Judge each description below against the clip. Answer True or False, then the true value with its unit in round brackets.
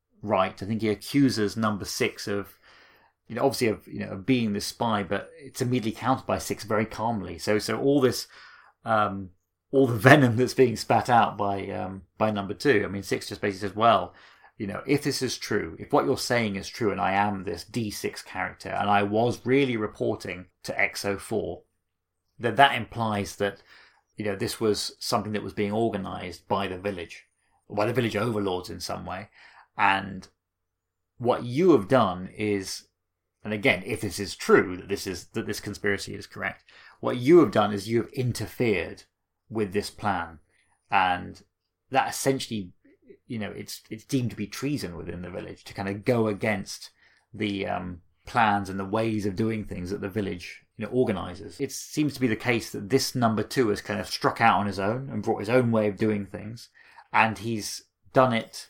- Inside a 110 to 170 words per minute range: False (200 wpm)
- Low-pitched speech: True (105 Hz)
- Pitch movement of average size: True (3.0 semitones)